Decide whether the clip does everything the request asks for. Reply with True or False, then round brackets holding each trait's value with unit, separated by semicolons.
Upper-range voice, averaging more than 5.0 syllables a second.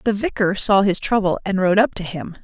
True (195 Hz; 5.4 syllables/s)